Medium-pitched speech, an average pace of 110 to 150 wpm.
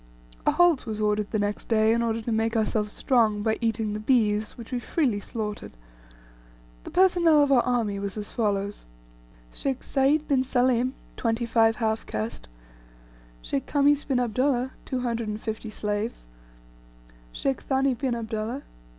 No: high, 225 Hz; average, 145 wpm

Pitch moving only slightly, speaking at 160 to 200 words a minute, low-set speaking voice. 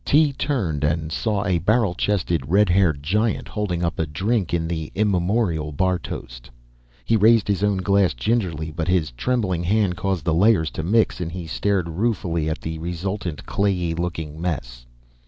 No: average, 4.2 semitones; average, 175 wpm; very low, 90 Hz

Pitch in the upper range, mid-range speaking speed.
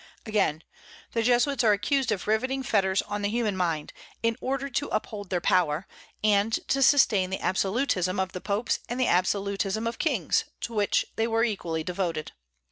Yes: high, 205 Hz; average, 175 wpm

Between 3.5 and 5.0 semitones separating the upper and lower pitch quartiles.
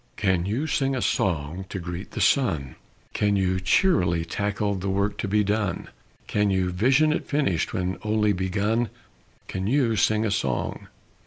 No: average, 3.0 semitones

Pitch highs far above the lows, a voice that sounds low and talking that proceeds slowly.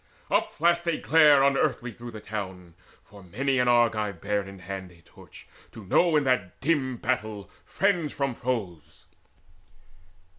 No: wide, 5.8 semitones; low, 120 Hz; average, 145 wpm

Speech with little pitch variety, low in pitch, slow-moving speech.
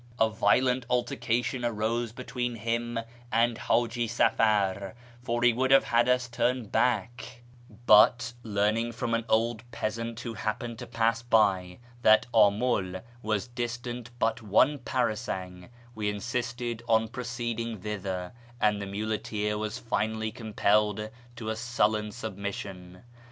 Yes: narrow, 2.1 semitones; low, 115 Hz; slow, 130 wpm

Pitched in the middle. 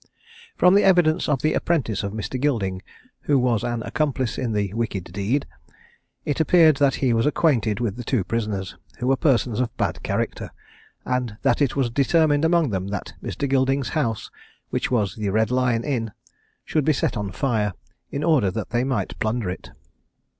No: low, 125 Hz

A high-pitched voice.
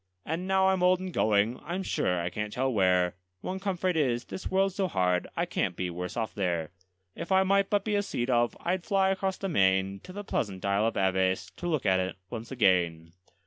No: low, 120 Hz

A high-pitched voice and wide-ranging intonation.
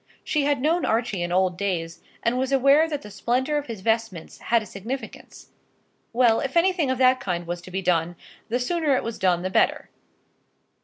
Yes: high, 230 Hz; wide, 6.6 semitones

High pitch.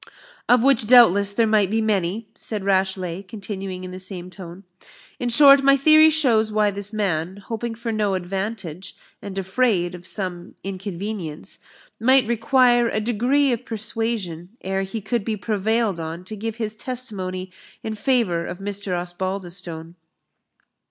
Yes: high, 205 Hz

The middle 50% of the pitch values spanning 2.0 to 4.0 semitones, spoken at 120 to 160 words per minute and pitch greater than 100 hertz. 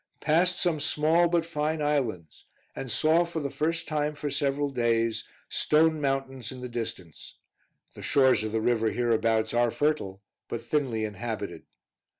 No: average, 5.0 semitones; average, 155 wpm; low, 135 Hz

